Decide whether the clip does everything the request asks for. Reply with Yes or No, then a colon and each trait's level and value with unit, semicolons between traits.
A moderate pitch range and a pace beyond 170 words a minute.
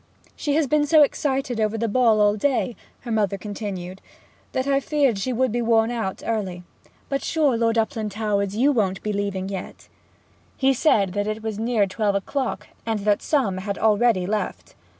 Yes: average, 4.0 semitones; average, 180 wpm